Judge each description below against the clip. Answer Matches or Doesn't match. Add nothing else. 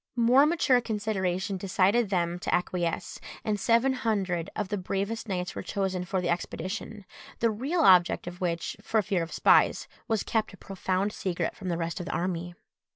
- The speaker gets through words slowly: Doesn't match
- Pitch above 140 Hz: Matches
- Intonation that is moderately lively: Matches